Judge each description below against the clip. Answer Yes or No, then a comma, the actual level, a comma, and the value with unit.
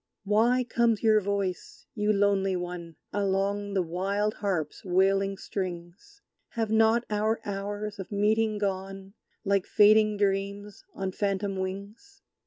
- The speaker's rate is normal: No, slow, 125 wpm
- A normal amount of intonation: No, narrow, 1.7 semitones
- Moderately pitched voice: No, high, 200 Hz